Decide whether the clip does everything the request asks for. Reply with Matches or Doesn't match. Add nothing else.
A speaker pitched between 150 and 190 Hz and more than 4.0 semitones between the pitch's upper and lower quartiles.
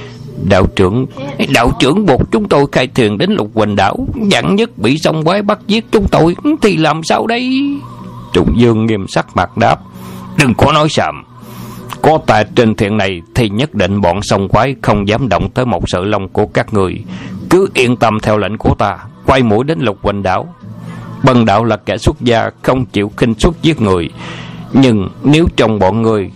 Doesn't match